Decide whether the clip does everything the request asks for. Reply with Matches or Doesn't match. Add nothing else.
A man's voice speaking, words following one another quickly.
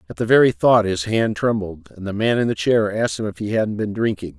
Matches